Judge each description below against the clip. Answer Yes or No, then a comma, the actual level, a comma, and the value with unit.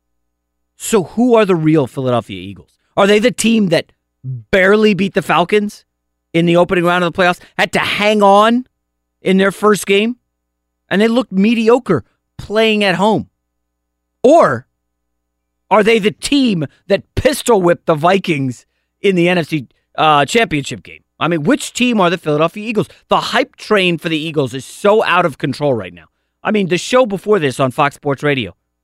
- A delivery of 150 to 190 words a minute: Yes, average, 175 wpm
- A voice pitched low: No, medium, 170 Hz